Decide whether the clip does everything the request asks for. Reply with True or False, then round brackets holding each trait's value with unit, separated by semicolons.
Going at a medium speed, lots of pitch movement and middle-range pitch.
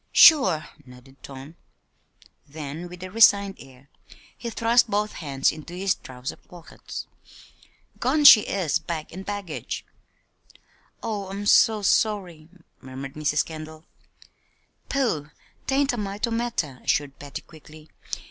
False (125 wpm; 6.1 semitones; 175 Hz)